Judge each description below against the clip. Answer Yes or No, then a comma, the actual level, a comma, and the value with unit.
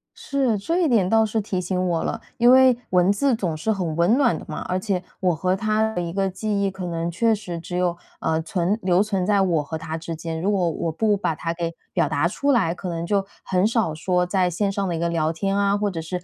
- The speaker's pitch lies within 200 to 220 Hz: No, medium, 185 Hz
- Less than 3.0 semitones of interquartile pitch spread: No, average, 3.6 semitones